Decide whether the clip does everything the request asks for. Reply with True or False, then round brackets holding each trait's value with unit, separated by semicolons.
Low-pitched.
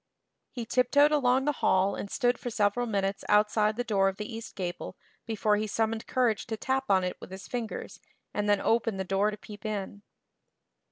False (215 Hz)